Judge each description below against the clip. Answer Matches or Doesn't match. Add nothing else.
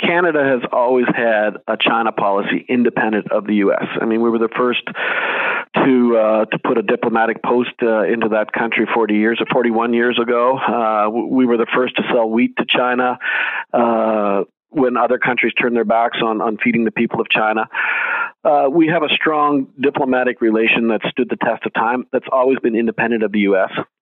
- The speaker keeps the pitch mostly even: Matches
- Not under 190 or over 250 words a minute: Matches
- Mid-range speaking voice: Doesn't match